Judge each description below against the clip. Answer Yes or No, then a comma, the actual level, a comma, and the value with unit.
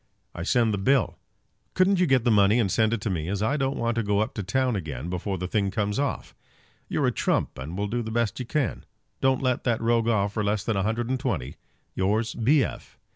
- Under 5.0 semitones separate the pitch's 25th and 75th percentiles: Yes, average, 3.6 semitones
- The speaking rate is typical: No, fast, 240 wpm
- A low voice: Yes, low, 110 Hz